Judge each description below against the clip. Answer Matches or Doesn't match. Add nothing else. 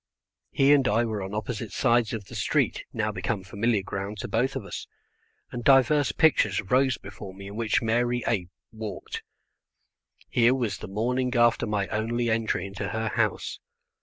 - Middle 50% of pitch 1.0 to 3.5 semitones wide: Matches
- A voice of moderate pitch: Doesn't match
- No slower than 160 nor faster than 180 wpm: Matches